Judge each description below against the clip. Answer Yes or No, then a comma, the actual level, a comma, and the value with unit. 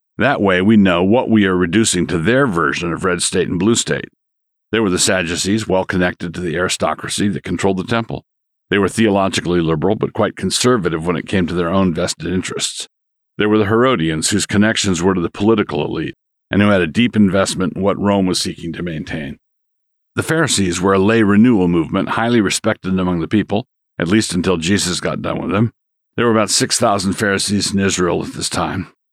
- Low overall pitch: Yes, very low, 95 Hz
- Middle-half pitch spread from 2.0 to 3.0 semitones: No, average, 3.4 semitones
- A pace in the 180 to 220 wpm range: Yes, fast, 205 wpm